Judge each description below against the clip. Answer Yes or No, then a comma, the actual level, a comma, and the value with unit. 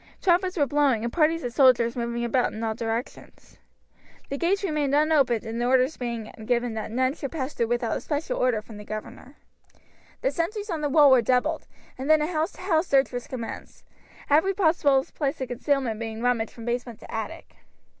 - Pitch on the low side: No, very high, 260 Hz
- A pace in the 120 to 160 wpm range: No, average, 195 wpm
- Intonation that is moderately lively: Yes, average, 4.6 semitones